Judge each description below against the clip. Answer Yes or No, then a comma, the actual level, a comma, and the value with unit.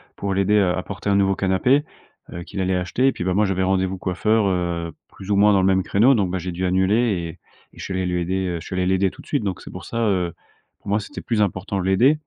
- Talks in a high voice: No, very low, 95 Hz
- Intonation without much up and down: Yes, narrow, 2.0 semitones